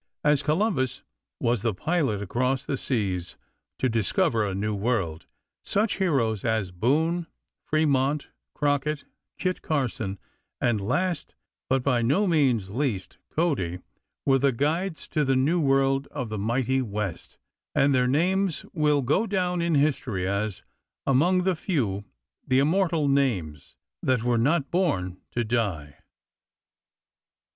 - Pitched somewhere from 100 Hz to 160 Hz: Yes, low, 135 Hz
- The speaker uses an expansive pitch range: Yes, wide, 5.9 semitones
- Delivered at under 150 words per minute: Yes, slow, 135 wpm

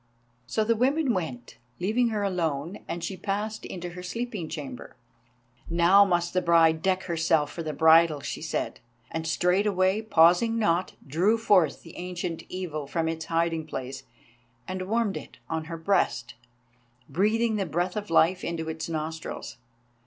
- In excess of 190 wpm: No, average, 155 wpm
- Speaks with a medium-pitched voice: Yes, medium, 175 Hz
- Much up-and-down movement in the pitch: No, average, 3.6 semitones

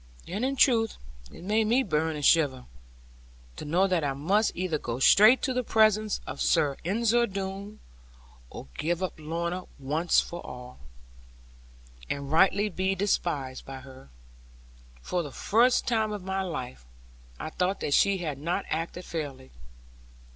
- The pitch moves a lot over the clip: Yes, wide, 5.8 semitones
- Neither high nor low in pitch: Yes, medium, 180 Hz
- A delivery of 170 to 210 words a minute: No, average, 155 wpm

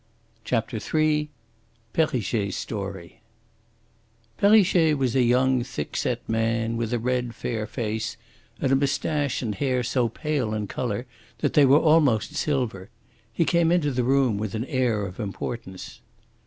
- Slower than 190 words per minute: Yes, average, 145 wpm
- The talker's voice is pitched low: Yes, low, 125 Hz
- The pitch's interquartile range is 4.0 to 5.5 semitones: Yes, average, 4.5 semitones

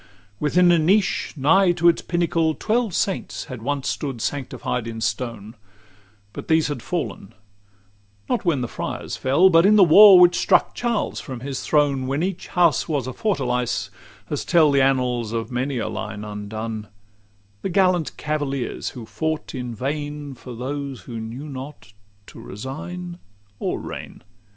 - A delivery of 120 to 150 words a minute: No, average, 165 wpm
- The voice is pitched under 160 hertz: Yes, medium, 140 Hz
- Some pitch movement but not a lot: No, wide, 5.8 semitones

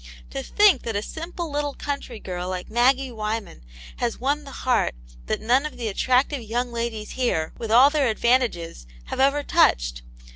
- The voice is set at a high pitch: Yes, high, 240 Hz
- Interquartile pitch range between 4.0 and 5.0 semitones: Yes, average, 4.4 semitones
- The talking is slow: No, average, 175 wpm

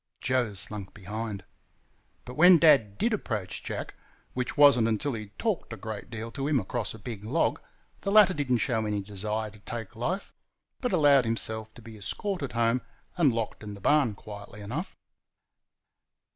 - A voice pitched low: Yes, low, 115 Hz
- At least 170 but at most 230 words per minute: Yes, average, 180 wpm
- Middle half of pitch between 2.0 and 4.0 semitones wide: No, average, 5.2 semitones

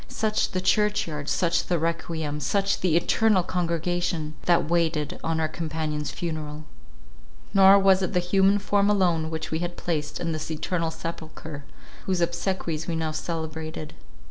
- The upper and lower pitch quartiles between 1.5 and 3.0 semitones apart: Yes, average, 2.7 semitones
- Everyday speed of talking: Yes, average, 155 wpm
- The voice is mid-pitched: Yes, medium, 165 Hz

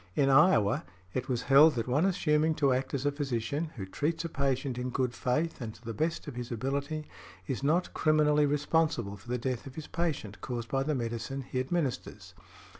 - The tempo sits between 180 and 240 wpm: Yes, average, 200 wpm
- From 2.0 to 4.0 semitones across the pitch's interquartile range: Yes, average, 3.7 semitones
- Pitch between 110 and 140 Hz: Yes, low, 135 Hz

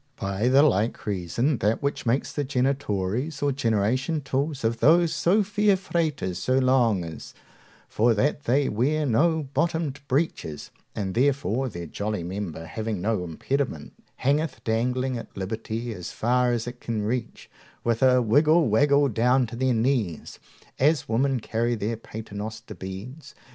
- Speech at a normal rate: Yes, average, 150 wpm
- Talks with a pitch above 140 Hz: No, low, 120 Hz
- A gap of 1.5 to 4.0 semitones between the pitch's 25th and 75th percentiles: No, average, 4.6 semitones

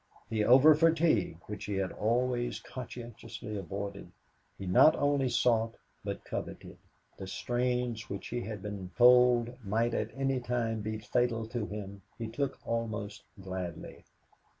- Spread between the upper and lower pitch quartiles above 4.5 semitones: No, average, 3.2 semitones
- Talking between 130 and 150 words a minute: Yes, average, 140 wpm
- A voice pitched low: Yes, low, 115 Hz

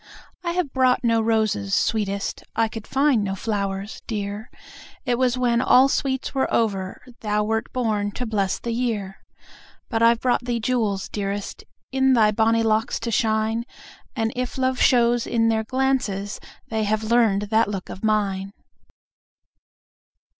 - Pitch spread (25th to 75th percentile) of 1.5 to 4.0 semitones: Yes, average, 2.9 semitones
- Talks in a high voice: Yes, high, 225 Hz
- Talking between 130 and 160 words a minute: Yes, average, 155 wpm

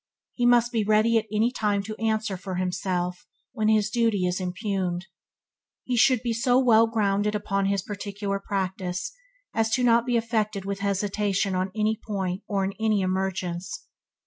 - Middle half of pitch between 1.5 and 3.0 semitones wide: Yes, narrow, 2.6 semitones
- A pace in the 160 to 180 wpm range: Yes, average, 170 wpm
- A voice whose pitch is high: Yes, high, 205 Hz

